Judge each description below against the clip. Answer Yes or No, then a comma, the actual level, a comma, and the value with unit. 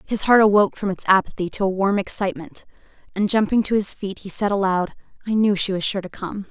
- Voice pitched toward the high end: Yes, high, 200 Hz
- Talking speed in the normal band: No, fast, 230 wpm